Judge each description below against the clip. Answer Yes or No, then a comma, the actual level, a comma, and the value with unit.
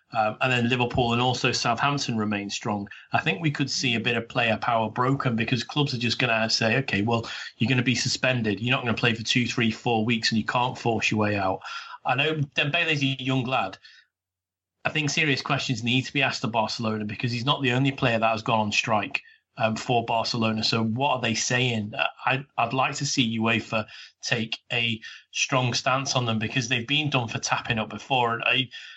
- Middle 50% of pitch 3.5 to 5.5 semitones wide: No, average, 2.8 semitones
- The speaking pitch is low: Yes, low, 120 Hz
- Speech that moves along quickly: Yes, fast, 225 wpm